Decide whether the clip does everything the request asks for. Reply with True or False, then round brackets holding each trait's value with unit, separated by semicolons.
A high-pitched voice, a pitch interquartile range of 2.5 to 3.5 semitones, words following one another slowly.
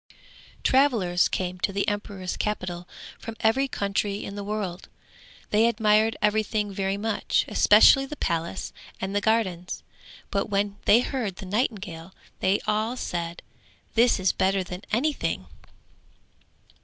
True (205 Hz; 2.8 semitones; 130 wpm)